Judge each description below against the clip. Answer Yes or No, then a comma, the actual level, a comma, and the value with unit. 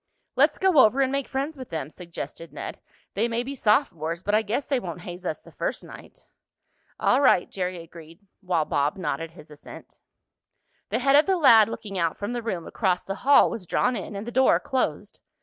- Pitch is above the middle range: Yes, high, 205 Hz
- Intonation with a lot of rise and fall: Yes, wide, 7.2 semitones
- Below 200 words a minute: No, fast, 205 wpm